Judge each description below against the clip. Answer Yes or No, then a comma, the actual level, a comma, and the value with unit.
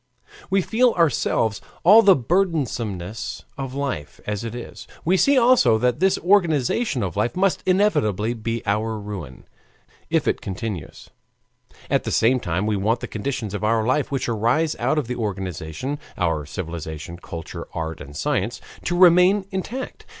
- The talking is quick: No, average, 155 wpm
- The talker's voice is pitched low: Yes, low, 115 Hz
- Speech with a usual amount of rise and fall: No, wide, 9.0 semitones